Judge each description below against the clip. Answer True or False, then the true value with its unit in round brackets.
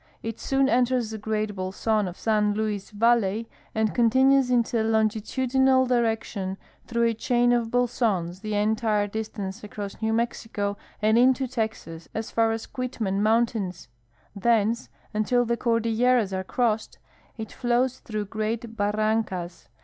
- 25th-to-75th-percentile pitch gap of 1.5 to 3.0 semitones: True (2.4 semitones)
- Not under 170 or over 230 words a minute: False (140 wpm)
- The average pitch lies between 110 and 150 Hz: False (220 Hz)